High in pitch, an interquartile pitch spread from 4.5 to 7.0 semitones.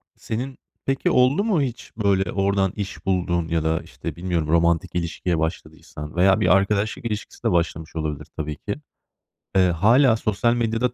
No: very low, 95 Hz; average, 5.1 semitones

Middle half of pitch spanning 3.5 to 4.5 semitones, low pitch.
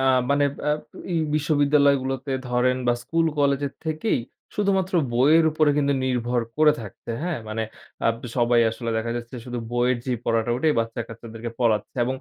Yes: average, 4.1 semitones; low, 130 Hz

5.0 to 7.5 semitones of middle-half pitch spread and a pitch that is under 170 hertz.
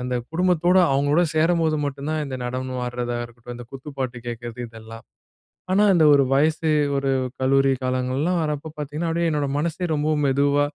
No: average, 3.7 semitones; medium, 140 Hz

